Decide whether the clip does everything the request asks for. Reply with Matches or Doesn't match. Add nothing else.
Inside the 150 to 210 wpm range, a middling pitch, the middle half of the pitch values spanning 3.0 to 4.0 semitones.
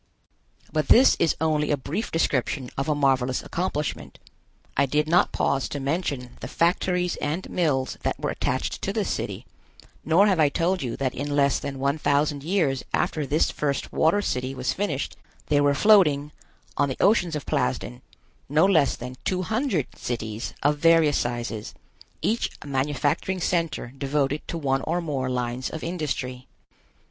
Matches